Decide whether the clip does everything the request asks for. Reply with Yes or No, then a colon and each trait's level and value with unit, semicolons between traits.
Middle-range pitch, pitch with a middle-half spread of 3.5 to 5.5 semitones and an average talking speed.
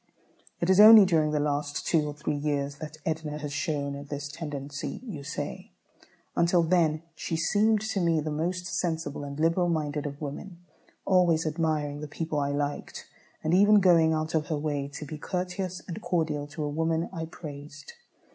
No: medium, 155 Hz; average, 2.9 semitones; average, 180 wpm